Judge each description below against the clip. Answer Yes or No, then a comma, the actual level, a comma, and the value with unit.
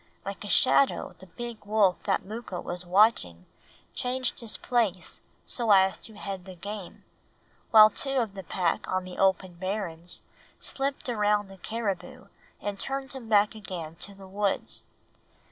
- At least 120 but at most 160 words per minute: Yes, average, 155 wpm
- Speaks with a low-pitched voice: No, high, 200 Hz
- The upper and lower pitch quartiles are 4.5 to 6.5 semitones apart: No, average, 3.1 semitones